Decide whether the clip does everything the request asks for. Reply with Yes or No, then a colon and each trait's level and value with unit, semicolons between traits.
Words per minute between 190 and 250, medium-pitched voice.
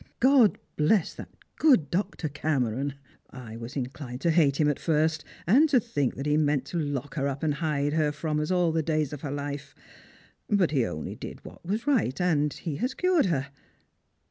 Yes: average, 200 wpm; medium, 150 Hz